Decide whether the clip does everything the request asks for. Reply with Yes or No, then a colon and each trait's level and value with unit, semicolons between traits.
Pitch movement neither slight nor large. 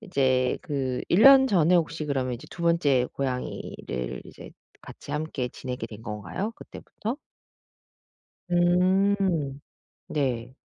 No: wide, 6.0 semitones